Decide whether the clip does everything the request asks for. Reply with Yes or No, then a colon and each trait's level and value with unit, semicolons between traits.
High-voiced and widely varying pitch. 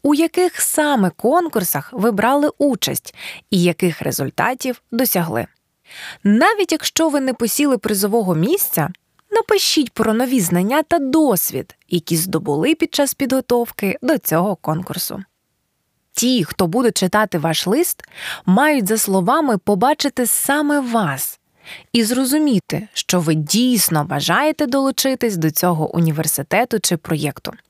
Yes: high, 225 Hz; wide, 7.9 semitones